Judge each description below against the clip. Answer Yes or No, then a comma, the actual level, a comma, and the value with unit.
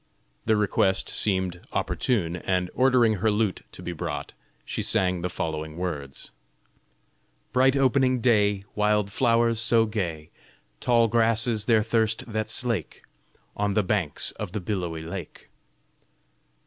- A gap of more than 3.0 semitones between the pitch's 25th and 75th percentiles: Yes, average, 4.2 semitones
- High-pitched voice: No, low, 105 Hz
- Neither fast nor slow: No, slow, 130 wpm